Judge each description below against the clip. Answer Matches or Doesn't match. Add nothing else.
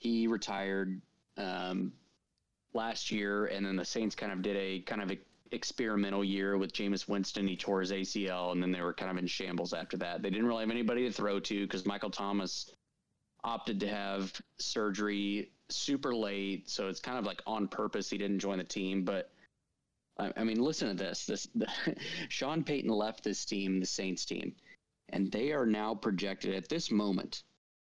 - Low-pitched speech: Matches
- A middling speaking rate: Matches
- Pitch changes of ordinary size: Doesn't match